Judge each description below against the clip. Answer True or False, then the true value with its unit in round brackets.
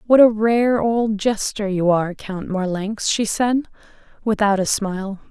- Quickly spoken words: False (160 wpm)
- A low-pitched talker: False (210 Hz)